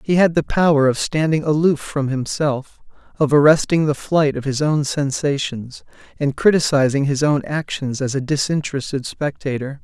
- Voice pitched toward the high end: No, medium, 145 Hz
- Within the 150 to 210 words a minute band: Yes, average, 160 wpm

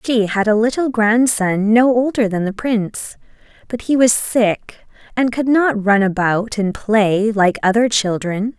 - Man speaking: No, female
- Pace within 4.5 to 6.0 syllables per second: No, 4.1 syllables/s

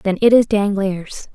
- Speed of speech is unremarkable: Yes, average, 180 wpm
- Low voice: No, high, 205 Hz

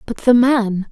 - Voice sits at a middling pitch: No, high, 230 Hz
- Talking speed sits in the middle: Yes, average, 195 wpm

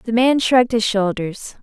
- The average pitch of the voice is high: Yes, high, 225 Hz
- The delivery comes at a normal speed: Yes, average, 185 wpm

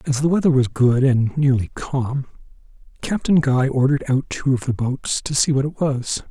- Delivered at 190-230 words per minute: Yes, average, 200 wpm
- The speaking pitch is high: No, low, 135 Hz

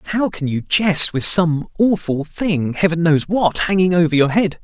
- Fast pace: No, average, 170 wpm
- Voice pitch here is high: No, medium, 170 Hz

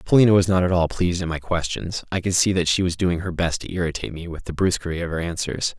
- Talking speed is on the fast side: Yes, fast, 280 wpm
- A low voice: Yes, very low, 85 Hz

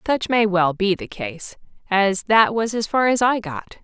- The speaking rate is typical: No, fast, 220 wpm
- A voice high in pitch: Yes, high, 205 Hz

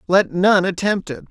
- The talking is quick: No, average, 185 wpm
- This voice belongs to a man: Yes, male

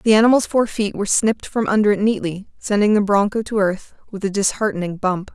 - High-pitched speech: Yes, high, 205 Hz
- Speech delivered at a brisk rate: Yes, fast, 215 wpm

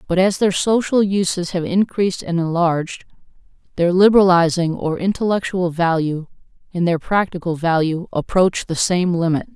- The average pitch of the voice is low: No, medium, 180 Hz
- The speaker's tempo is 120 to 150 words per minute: Yes, average, 140 wpm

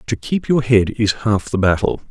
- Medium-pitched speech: No, low, 110 Hz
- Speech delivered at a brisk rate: Yes, fast, 230 wpm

